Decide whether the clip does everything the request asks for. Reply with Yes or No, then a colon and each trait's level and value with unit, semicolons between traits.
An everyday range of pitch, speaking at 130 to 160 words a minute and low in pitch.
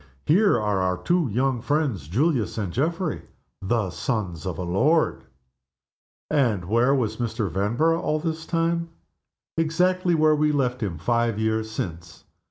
No: wide, 7.4 semitones; average, 145 wpm; low, 120 Hz